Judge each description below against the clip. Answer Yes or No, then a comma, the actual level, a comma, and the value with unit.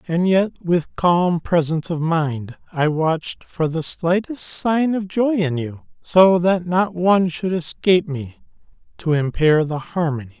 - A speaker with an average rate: Yes, average, 160 wpm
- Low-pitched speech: No, medium, 170 Hz